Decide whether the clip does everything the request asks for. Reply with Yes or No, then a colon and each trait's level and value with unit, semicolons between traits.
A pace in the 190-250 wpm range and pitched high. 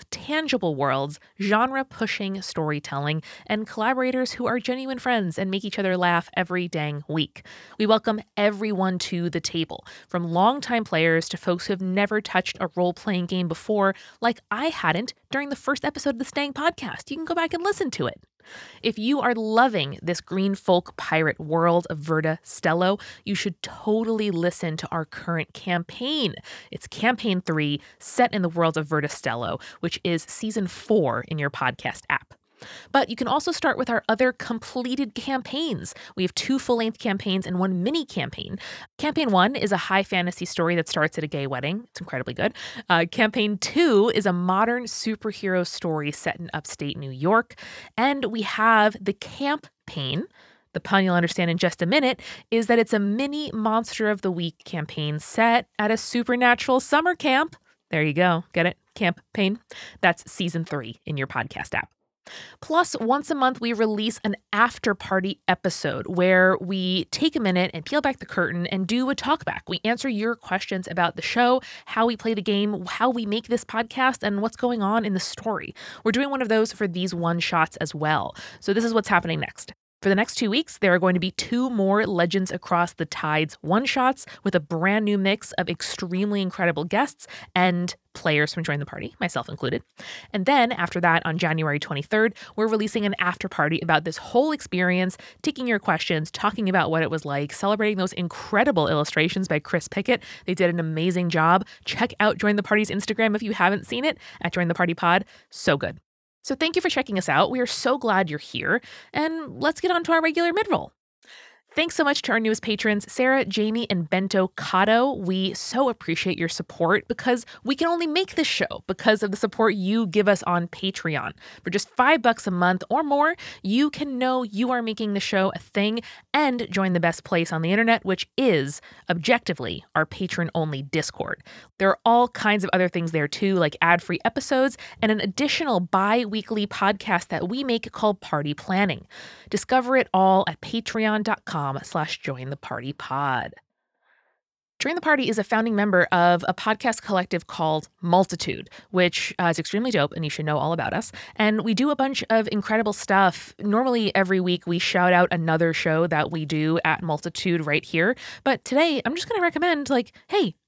Yes: average, 195 wpm; high, 200 Hz